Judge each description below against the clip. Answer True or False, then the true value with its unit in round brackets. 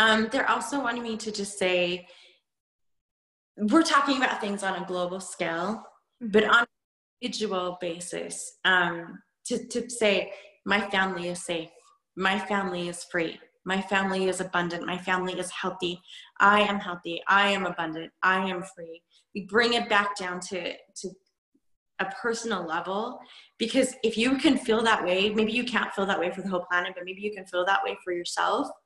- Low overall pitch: False (195 Hz)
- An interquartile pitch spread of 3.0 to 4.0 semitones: True (3.6 semitones)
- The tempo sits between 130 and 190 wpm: True (180 wpm)